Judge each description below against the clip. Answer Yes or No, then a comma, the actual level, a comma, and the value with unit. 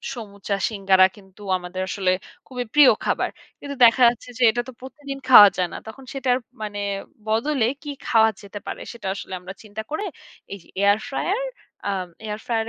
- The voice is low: No, high, 220 Hz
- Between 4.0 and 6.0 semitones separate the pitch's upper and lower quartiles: Yes, average, 4.4 semitones